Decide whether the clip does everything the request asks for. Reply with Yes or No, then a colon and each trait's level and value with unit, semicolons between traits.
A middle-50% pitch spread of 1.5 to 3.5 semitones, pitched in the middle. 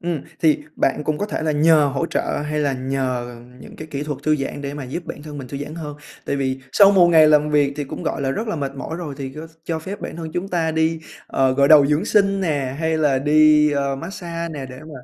Yes: average, 2.7 semitones; medium, 150 Hz